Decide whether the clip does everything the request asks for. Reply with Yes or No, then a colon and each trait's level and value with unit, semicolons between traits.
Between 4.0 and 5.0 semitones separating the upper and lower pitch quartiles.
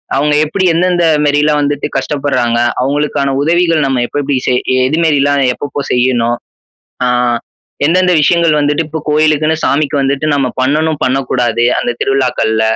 No: narrow, 2.6 semitones